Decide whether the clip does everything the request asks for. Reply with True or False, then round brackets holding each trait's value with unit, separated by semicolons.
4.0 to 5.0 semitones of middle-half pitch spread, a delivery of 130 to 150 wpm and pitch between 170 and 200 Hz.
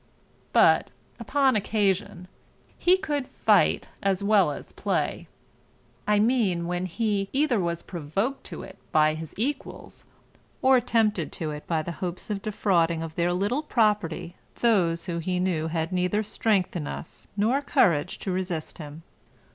True (4.4 semitones; 145 wpm; 185 Hz)